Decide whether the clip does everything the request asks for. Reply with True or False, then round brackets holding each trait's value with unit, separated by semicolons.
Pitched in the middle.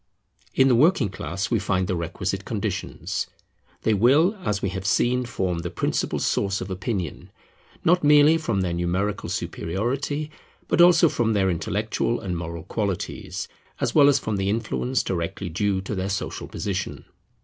False (100 Hz)